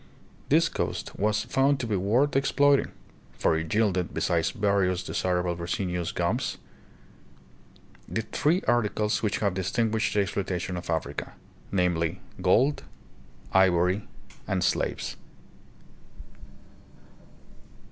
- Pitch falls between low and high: No, low, 100 Hz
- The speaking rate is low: Yes, slow, 105 wpm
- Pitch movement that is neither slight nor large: Yes, average, 3.9 semitones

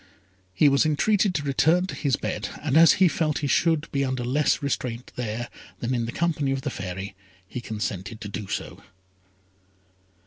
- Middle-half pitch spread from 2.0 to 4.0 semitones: No, average, 4.9 semitones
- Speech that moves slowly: No, average, 180 wpm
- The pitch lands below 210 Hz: Yes, low, 135 Hz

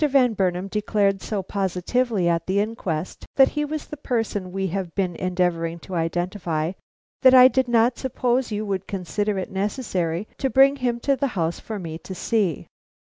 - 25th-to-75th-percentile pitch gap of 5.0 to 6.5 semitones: Yes, average, 5.3 semitones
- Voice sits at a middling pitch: No, high, 200 Hz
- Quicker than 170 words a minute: Yes, average, 180 wpm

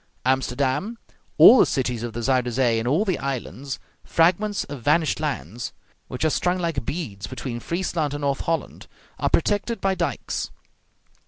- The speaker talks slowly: No, average, 160 wpm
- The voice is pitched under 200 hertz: Yes, medium, 140 Hz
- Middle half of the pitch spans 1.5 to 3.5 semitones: No, average, 5.3 semitones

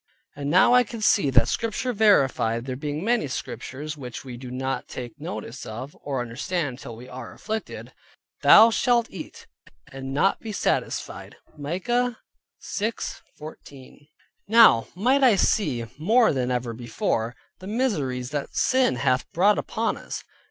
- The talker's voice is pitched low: No, medium, 145 Hz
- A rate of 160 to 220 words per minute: No, average, 145 wpm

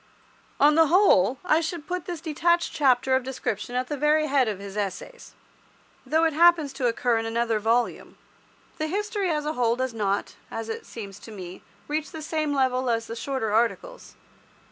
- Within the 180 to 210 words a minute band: Yes, average, 190 wpm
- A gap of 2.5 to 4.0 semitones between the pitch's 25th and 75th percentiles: No, wide, 5.6 semitones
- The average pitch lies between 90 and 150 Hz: No, very high, 265 Hz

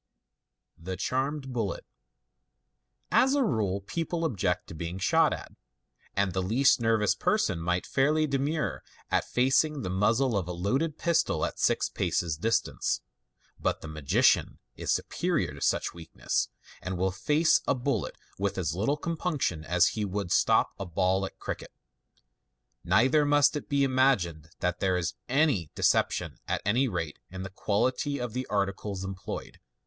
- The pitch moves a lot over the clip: Yes, wide, 7.1 semitones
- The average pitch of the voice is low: Yes, low, 105 Hz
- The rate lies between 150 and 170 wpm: Yes, average, 160 wpm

